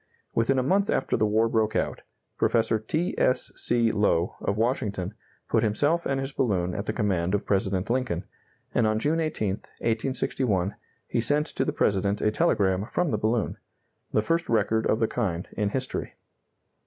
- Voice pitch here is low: Yes, low, 110 Hz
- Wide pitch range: No, average, 4.3 semitones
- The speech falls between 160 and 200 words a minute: Yes, average, 175 wpm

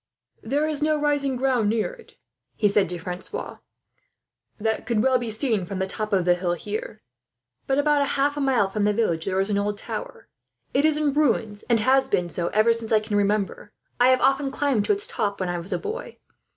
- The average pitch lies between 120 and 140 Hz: No, high, 225 Hz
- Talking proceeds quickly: Yes, fast, 225 wpm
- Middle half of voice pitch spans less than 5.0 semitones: No, wide, 5.6 semitones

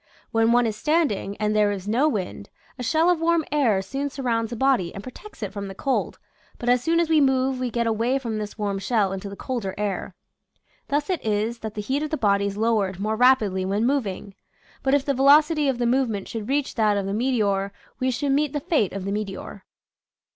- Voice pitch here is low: No, high, 230 Hz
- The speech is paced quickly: Yes, fast, 225 wpm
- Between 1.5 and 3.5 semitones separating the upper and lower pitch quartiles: No, average, 5.0 semitones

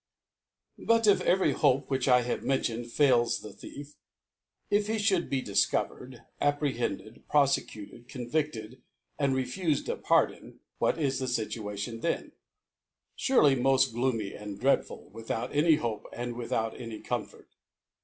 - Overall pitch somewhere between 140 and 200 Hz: No, low, 130 Hz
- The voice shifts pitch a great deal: No, average, 3.9 semitones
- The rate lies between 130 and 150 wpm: Yes, average, 145 wpm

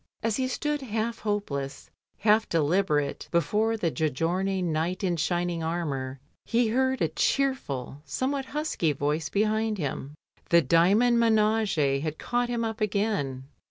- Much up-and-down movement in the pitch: Yes, wide, 6.3 semitones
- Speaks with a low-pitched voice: No, high, 190 Hz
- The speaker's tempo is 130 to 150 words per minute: Yes, average, 140 wpm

